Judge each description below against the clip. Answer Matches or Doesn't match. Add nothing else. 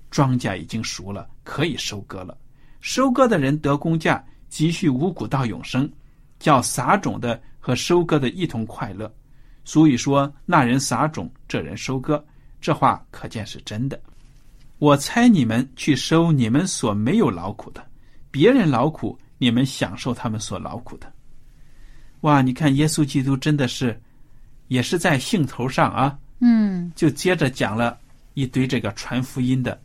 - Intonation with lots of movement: Doesn't match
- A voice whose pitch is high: Doesn't match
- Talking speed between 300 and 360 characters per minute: Doesn't match